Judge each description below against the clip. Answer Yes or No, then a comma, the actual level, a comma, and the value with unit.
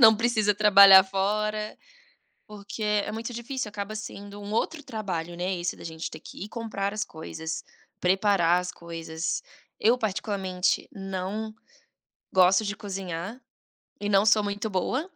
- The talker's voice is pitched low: No, high, 200 Hz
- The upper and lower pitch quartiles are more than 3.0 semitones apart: No, narrow, 2.6 semitones